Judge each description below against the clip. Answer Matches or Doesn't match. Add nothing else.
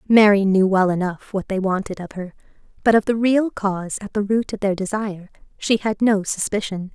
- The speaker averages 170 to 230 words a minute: Matches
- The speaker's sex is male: Doesn't match